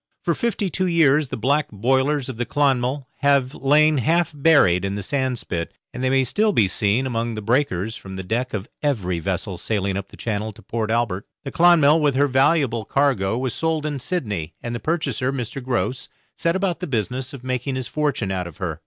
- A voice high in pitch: No, low, 130 Hz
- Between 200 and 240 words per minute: Yes, fast, 205 wpm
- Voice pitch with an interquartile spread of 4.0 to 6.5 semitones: Yes, average, 5.1 semitones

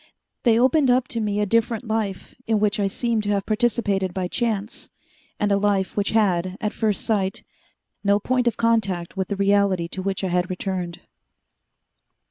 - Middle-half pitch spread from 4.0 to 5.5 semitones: No, average, 2.8 semitones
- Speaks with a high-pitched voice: Yes, high, 205 Hz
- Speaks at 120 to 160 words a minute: No, average, 180 wpm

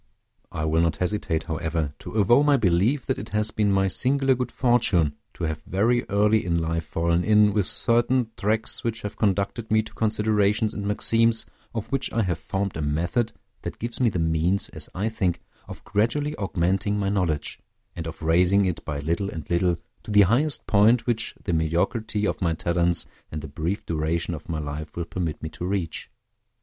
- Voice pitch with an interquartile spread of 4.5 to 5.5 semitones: Yes, average, 4.8 semitones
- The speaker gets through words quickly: No, average, 195 wpm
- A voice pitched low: Yes, low, 100 Hz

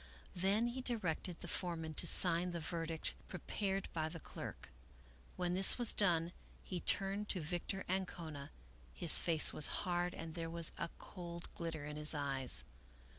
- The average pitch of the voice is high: No, medium, 170 Hz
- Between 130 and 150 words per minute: No, average, 165 wpm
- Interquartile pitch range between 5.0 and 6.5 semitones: No, average, 2.8 semitones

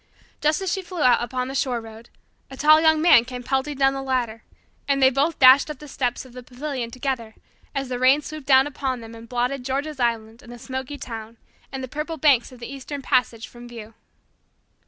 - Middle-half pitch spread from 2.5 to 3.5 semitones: Yes, average, 2.9 semitones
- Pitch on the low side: No, very high, 260 Hz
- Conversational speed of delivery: No, fast, 220 wpm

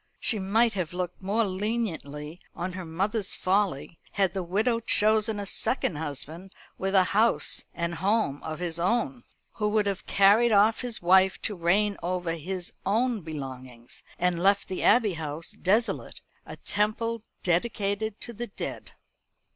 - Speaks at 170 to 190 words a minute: No, average, 155 wpm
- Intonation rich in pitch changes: No, average, 4.0 semitones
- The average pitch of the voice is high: Yes, high, 195 Hz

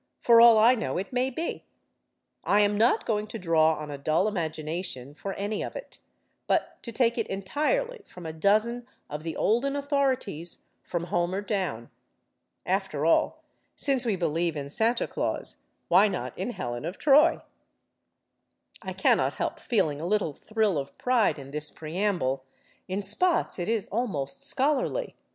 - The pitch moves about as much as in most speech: No, wide, 6.7 semitones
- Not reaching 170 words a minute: Yes, average, 160 wpm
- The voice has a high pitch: Yes, high, 200 Hz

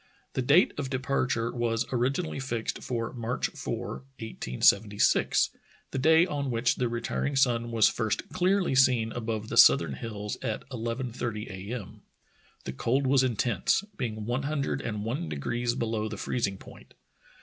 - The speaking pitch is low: Yes, low, 120 Hz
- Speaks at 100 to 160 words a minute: Yes, average, 155 wpm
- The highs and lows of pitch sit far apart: No, average, 3.0 semitones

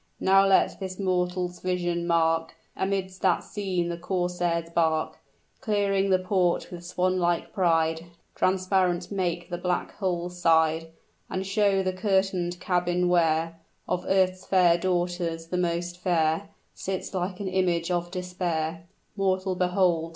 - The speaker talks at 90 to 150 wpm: Yes, slow, 135 wpm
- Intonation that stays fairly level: Yes, narrow, 1.6 semitones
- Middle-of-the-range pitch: Yes, medium, 180 Hz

